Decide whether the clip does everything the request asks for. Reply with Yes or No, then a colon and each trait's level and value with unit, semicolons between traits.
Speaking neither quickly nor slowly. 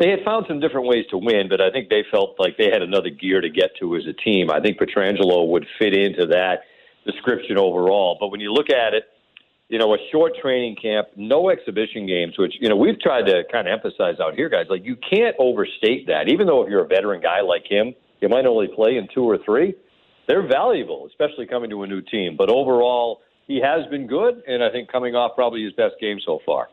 No: fast, 240 wpm